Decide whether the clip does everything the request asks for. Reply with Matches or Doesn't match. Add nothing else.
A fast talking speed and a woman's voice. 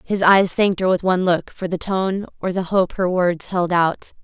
Matches